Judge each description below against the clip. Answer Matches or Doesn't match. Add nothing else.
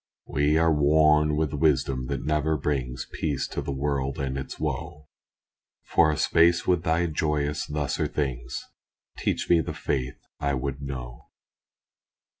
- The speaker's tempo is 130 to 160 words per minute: Matches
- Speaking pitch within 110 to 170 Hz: Doesn't match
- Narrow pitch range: Matches